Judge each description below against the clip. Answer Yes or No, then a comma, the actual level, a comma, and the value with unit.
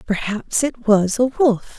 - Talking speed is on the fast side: No, average, 170 wpm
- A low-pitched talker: No, high, 230 Hz